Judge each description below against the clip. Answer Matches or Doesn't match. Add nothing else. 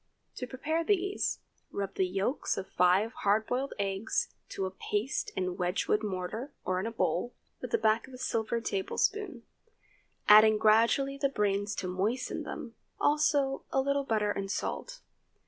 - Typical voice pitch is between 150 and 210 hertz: Doesn't match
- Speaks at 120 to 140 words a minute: Doesn't match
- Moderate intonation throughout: Doesn't match